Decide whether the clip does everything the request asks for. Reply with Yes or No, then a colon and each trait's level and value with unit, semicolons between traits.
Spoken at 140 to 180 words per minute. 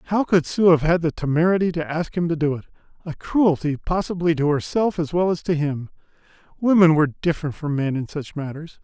No: fast, 205 wpm